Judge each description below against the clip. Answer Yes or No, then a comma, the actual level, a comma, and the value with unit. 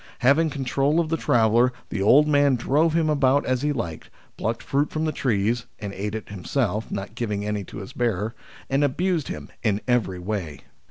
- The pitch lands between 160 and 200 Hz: No, low, 125 Hz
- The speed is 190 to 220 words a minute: Yes, average, 200 wpm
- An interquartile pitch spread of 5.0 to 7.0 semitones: Yes, wide, 5.5 semitones